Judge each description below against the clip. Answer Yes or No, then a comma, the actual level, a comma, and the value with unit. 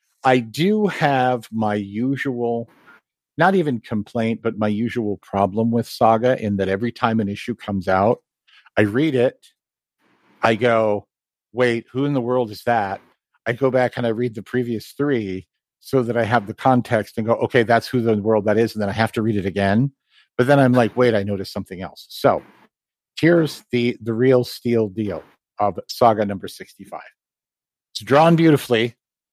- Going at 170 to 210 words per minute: Yes, average, 180 wpm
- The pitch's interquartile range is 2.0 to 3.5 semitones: Yes, narrow, 2.6 semitones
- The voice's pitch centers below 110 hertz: No, low, 115 Hz